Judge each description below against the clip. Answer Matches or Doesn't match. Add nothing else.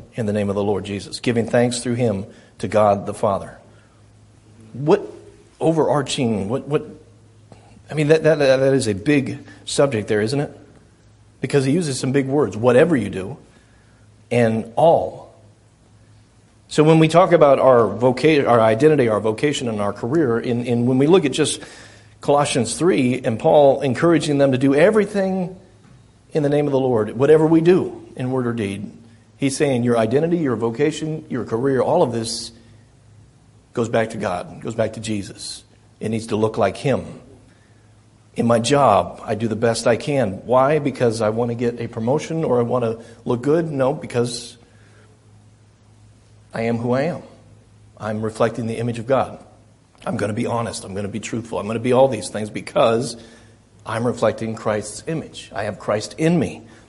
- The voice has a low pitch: Matches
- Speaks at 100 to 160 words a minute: Doesn't match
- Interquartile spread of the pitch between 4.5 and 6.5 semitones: Doesn't match